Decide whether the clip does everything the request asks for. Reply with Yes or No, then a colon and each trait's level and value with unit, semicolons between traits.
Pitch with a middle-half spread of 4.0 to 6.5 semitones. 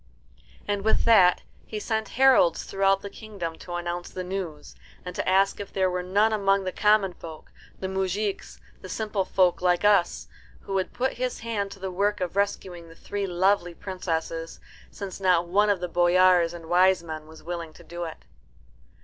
No: narrow, 2.5 semitones